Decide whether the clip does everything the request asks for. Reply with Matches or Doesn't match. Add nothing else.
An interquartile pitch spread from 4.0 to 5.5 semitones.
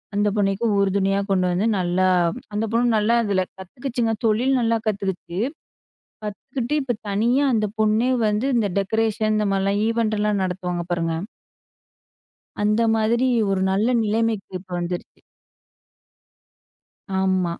Doesn't match